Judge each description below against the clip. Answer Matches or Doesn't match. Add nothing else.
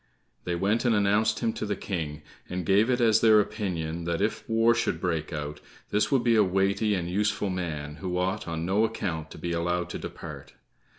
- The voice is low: Matches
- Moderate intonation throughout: Matches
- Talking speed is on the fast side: Matches